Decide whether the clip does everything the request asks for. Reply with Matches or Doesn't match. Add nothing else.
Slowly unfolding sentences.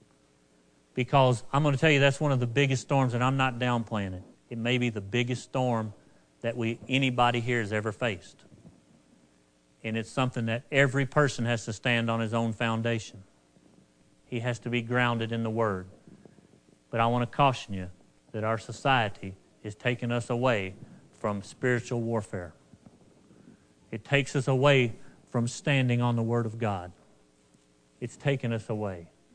Doesn't match